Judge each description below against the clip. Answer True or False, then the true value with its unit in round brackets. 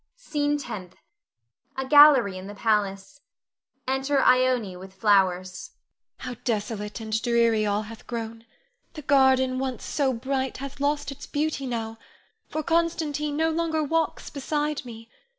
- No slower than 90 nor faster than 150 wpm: True (140 wpm)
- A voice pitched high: True (255 Hz)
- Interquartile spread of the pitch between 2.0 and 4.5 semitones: False (4.9 semitones)